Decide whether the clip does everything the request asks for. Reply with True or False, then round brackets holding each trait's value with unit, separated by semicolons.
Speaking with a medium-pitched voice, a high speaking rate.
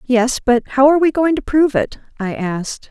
False (260 Hz; 225 wpm)